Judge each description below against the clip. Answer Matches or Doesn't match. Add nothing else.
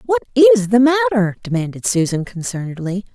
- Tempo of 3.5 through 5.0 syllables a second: Doesn't match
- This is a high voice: Matches